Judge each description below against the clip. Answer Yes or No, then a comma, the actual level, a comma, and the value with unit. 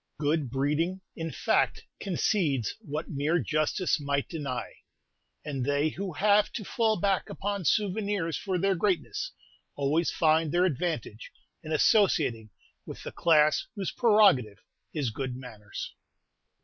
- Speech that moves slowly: Yes, slow, 130 wpm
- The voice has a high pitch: No, medium, 160 Hz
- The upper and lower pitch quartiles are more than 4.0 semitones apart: Yes, average, 5.2 semitones